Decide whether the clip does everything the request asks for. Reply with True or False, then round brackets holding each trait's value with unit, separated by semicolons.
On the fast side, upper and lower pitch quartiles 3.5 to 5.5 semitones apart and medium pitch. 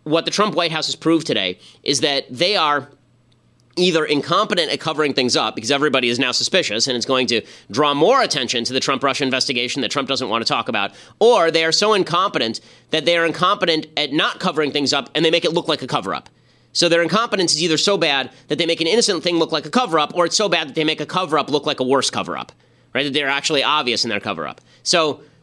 True (245 wpm; 4.1 semitones; 150 Hz)